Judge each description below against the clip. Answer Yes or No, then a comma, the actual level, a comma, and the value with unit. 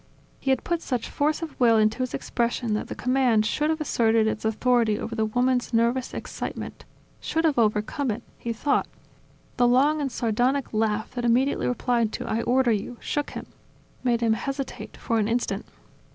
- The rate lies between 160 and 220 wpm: Yes, average, 180 wpm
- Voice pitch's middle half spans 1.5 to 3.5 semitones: Yes, average, 3.0 semitones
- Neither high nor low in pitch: No, high, 240 Hz